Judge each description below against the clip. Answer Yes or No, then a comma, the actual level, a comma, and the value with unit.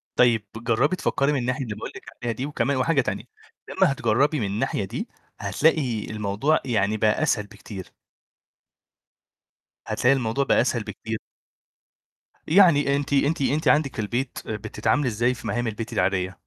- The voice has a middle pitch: No, low, 120 Hz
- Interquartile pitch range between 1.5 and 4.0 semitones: No, average, 4.4 semitones